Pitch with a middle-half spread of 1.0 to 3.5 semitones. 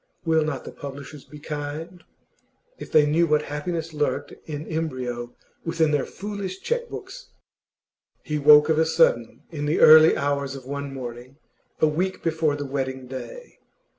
Yes: narrow, 2.5 semitones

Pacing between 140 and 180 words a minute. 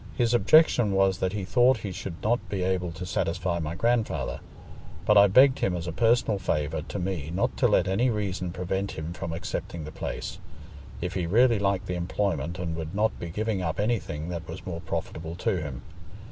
No: average, 200 wpm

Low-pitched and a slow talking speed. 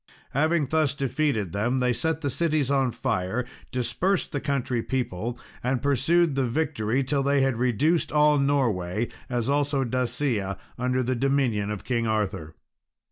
No: low, 130 Hz; average, 150 wpm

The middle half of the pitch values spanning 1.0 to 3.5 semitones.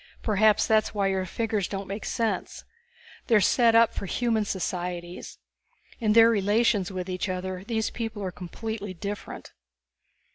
Yes: average, 3.0 semitones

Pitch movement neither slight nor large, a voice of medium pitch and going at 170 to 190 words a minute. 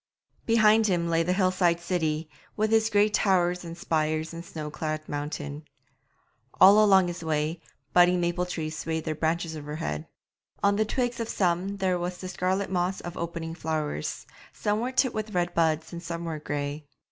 Yes: average, 3.3 semitones; medium, 175 Hz; average, 180 wpm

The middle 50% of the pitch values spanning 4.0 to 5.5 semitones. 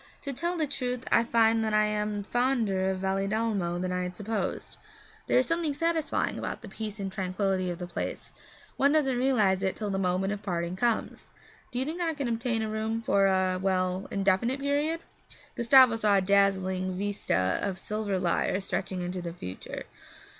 Yes: average, 4.4 semitones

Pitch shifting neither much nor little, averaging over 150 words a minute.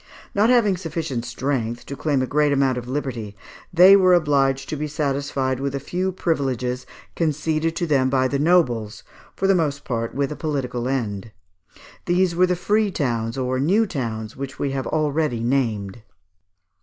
Yes: average, 4.5 semitones; average, 170 wpm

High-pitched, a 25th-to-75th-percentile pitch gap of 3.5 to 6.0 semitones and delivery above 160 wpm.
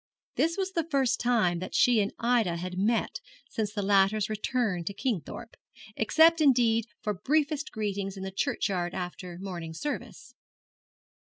No: high, 215 Hz; average, 4.9 semitones; average, 150 wpm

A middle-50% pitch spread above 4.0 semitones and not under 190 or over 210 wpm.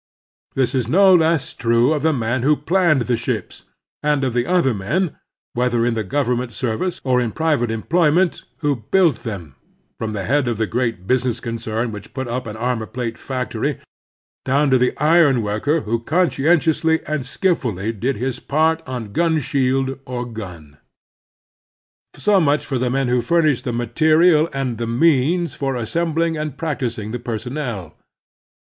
No: average, 4.8 semitones; average, 165 wpm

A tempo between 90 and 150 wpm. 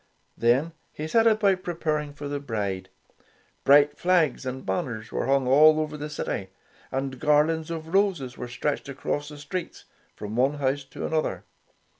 No: average, 160 wpm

